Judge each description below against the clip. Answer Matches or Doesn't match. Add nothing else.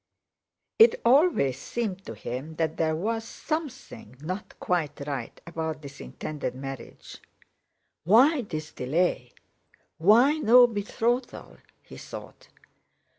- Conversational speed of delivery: Doesn't match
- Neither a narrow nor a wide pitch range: Doesn't match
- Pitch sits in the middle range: Matches